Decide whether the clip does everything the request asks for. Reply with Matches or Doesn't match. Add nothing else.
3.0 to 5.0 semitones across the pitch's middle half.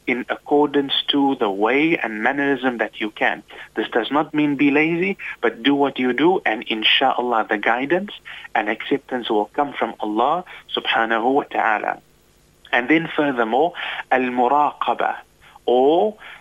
Matches